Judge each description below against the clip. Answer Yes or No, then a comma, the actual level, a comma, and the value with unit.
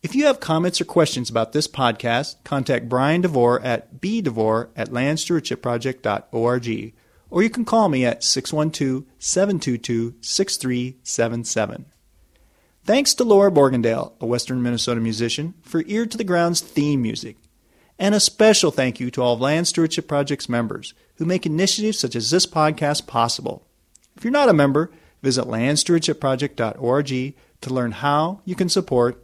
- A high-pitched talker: No, medium, 140 Hz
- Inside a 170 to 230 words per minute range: No, average, 150 wpm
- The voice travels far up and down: Yes, wide, 6.0 semitones